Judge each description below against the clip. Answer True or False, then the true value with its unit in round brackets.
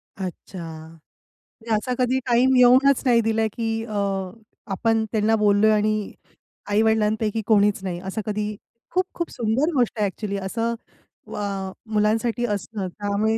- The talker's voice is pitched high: True (220 Hz)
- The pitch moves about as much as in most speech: False (2.2 semitones)